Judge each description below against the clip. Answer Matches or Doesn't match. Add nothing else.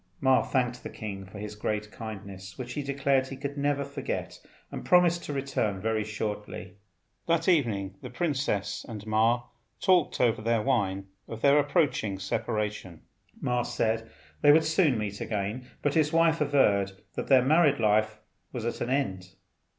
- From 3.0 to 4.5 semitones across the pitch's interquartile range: Doesn't match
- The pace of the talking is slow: Doesn't match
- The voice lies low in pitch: Matches